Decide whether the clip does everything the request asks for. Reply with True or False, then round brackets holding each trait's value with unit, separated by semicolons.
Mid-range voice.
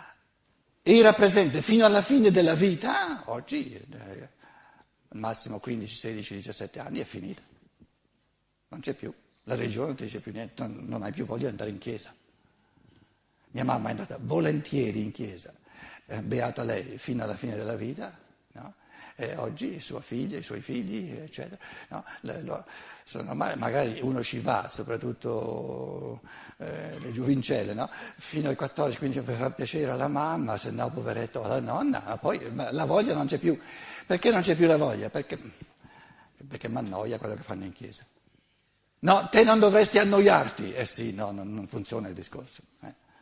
False (130 Hz)